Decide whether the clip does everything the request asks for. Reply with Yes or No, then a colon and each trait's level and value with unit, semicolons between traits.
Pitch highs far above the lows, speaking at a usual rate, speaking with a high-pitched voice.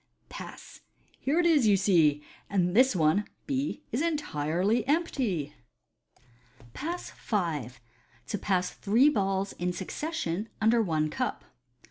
No: wide, 7.5 semitones; slow, 120 wpm; high, 200 Hz